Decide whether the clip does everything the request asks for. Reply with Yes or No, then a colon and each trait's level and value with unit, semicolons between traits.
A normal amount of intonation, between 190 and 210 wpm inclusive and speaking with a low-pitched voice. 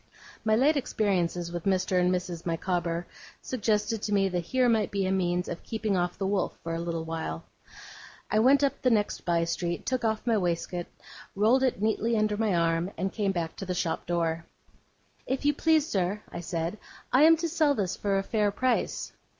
No: average, 4.4 semitones; average, 200 wpm; high, 195 Hz